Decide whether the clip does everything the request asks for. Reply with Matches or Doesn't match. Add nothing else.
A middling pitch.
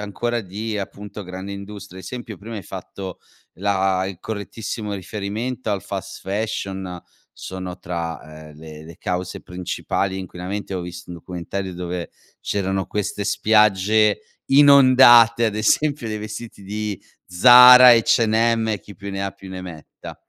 Doesn't match